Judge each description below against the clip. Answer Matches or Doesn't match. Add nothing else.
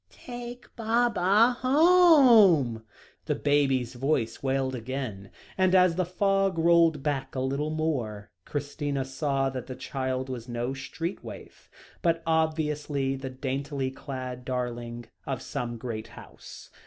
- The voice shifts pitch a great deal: Doesn't match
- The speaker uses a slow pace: Matches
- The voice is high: Doesn't match